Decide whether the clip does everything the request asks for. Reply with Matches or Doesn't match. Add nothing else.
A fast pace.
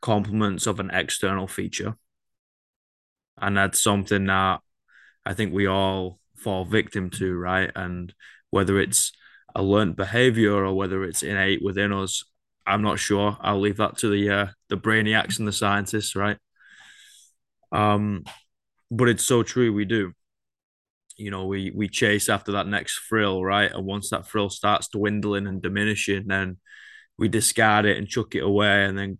Doesn't match